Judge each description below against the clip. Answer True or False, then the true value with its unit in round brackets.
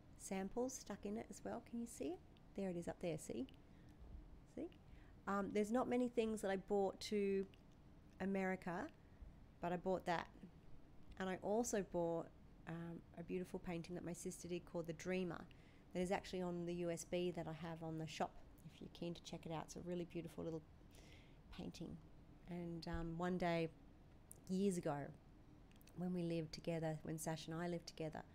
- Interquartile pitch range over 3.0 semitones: False (2.6 semitones)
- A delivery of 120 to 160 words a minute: False (185 wpm)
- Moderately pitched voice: True (175 Hz)